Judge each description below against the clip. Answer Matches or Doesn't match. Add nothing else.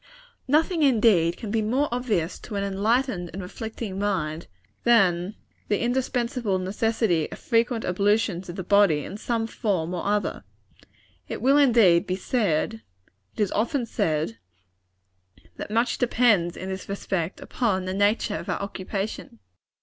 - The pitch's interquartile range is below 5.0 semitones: Matches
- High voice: Matches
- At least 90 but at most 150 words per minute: Matches